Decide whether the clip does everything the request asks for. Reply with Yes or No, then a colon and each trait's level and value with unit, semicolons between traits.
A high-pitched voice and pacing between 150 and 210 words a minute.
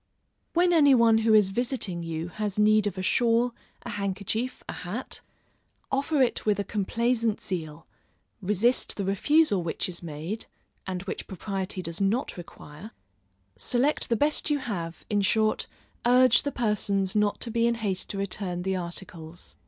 Yes: high, 210 Hz; average, 160 wpm